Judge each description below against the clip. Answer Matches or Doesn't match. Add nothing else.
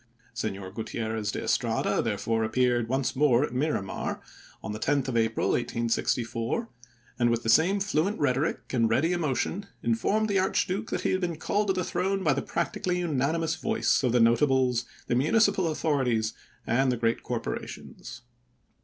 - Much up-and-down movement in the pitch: Matches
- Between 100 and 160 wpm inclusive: Doesn't match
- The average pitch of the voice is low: Matches